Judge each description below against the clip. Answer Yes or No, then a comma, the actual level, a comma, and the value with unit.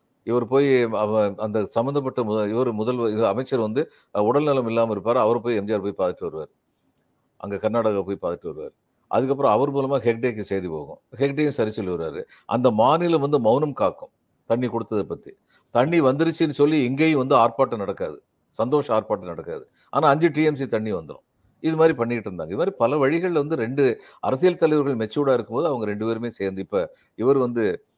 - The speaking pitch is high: No, low, 125 Hz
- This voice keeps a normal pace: No, fast, 165 wpm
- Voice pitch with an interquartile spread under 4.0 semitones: No, average, 4.9 semitones